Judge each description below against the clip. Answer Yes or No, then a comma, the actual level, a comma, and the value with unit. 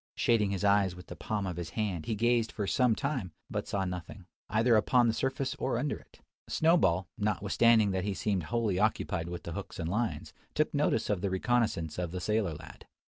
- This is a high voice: No, low, 105 Hz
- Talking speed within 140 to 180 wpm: No, fast, 205 wpm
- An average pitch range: Yes, average, 4.2 semitones